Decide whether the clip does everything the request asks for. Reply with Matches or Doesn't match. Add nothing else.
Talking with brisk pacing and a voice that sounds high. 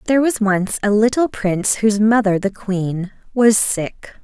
Doesn't match